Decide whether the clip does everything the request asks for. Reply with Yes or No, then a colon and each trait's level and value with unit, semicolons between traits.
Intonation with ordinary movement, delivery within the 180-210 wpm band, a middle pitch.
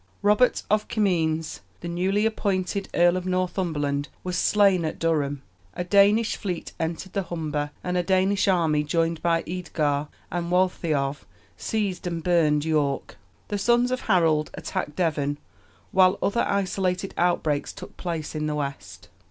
No: average, 3.6 semitones; average, 145 wpm; medium, 175 Hz